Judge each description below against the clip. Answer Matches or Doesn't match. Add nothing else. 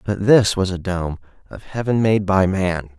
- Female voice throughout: Doesn't match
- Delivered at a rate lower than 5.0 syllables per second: Matches